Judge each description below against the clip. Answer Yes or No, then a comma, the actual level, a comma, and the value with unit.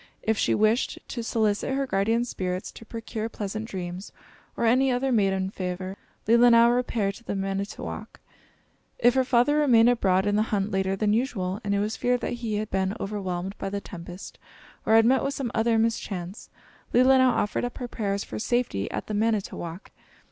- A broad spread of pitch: No, average, 3.6 semitones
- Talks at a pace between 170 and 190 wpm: Yes, average, 185 wpm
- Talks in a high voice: Yes, high, 215 Hz